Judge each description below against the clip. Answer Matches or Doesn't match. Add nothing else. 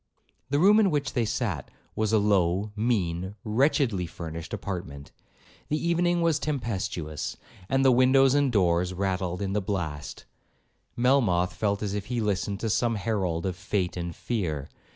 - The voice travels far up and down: Matches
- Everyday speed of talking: Matches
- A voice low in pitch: Matches